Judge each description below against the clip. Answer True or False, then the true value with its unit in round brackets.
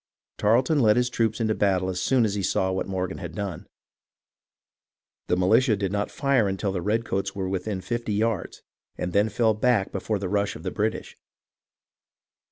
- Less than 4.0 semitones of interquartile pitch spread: True (2.9 semitones)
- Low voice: True (100 Hz)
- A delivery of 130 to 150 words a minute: False (175 wpm)